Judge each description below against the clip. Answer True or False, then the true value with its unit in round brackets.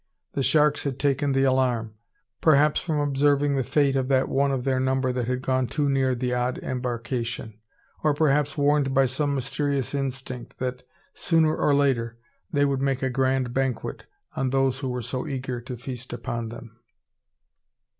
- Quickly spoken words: False (175 wpm)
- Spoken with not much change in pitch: True (2.0 semitones)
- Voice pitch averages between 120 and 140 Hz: True (135 Hz)